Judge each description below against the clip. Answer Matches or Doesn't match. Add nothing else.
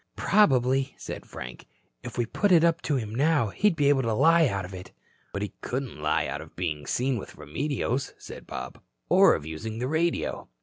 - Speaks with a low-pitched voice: Matches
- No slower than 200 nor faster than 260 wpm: Matches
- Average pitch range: Doesn't match